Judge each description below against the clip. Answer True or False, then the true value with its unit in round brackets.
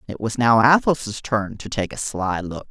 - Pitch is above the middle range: False (110 Hz)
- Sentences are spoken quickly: True (220 wpm)